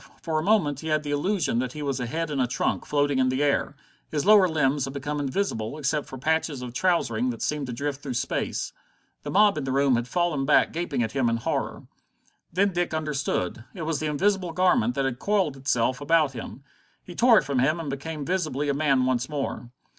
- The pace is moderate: No, fast, 225 wpm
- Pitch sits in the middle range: Yes, medium, 145 Hz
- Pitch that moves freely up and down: No, average, 3.7 semitones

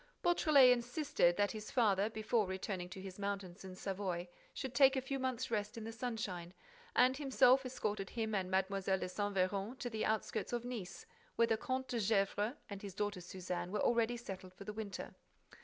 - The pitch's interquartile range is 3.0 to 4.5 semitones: Yes, average, 4.1 semitones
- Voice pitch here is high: Yes, high, 210 Hz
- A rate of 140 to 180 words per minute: No, average, 195 wpm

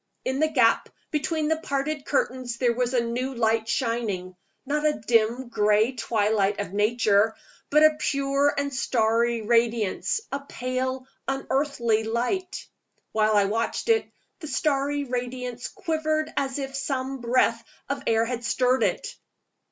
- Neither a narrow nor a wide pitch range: Yes, average, 3.5 semitones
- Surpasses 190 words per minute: No, average, 145 wpm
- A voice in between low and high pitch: No, very high, 250 Hz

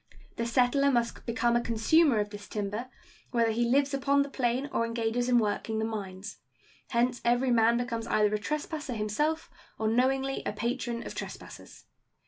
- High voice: Yes, high, 235 Hz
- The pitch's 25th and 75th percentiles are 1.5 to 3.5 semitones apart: Yes, average, 2.9 semitones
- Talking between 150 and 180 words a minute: Yes, average, 170 wpm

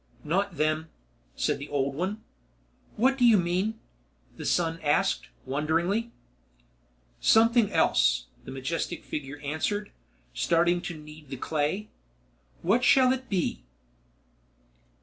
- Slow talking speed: Yes, slow, 115 wpm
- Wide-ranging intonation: Yes, wide, 5.8 semitones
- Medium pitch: Yes, medium, 170 Hz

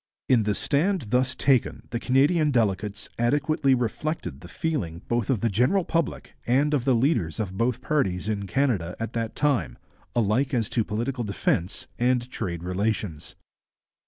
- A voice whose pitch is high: No, low, 120 Hz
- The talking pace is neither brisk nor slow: Yes, average, 160 wpm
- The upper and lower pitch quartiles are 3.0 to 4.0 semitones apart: No, average, 5.1 semitones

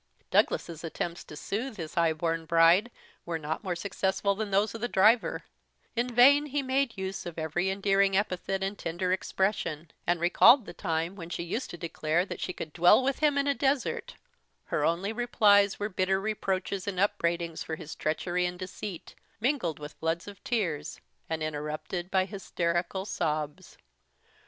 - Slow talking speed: No, average, 170 wpm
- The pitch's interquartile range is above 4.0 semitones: No, average, 3.7 semitones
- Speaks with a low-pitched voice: No, medium, 185 Hz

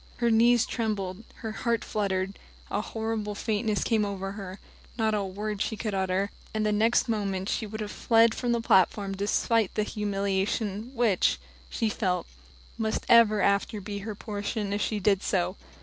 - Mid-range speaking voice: No, high, 210 Hz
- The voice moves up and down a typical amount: No, narrow, 2.1 semitones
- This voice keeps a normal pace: Yes, average, 170 wpm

